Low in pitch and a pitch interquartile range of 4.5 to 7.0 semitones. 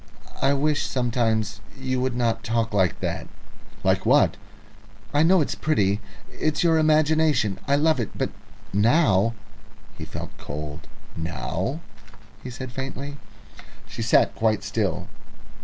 Yes: low, 120 Hz; wide, 5.5 semitones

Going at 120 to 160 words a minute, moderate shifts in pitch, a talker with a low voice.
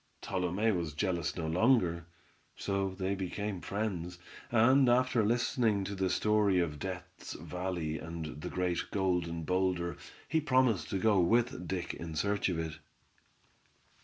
Yes: average, 140 wpm; average, 3.6 semitones; very low, 95 Hz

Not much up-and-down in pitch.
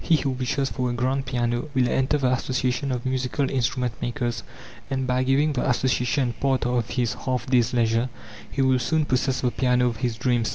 Yes: narrow, 1.5 semitones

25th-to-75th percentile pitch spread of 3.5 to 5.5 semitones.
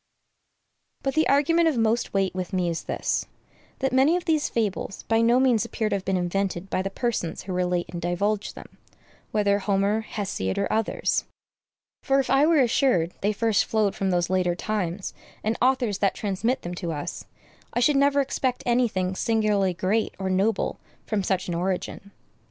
Yes: average, 4.5 semitones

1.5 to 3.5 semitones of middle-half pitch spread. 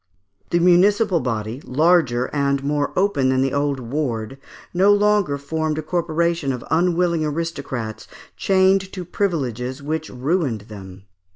No: average, 5.2 semitones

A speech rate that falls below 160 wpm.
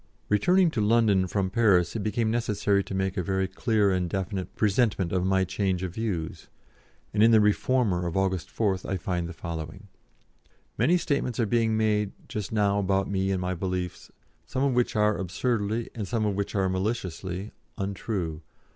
No: average, 180 wpm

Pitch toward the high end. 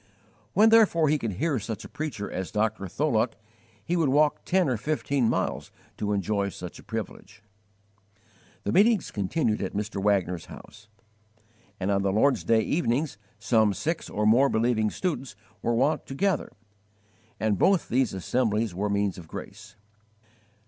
No: low, 115 Hz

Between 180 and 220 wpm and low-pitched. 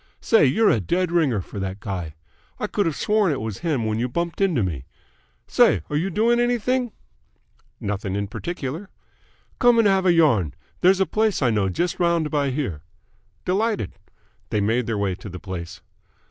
No: average, 185 wpm; medium, 145 Hz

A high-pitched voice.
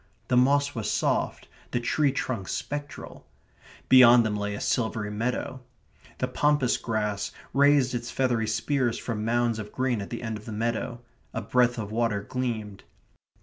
No: low, 120 Hz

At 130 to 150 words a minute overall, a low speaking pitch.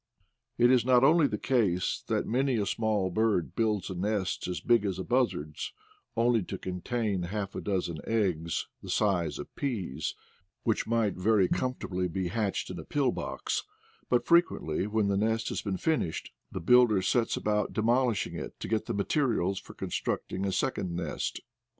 No: average, 175 wpm; low, 105 Hz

